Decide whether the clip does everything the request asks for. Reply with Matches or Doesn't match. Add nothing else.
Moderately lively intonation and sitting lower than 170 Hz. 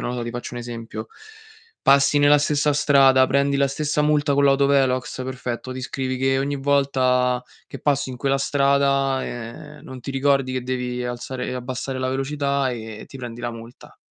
Doesn't match